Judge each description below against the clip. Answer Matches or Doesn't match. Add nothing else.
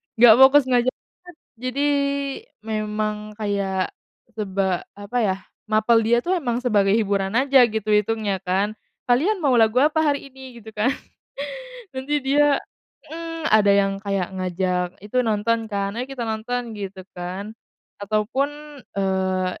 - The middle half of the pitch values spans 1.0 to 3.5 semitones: Doesn't match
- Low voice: Doesn't match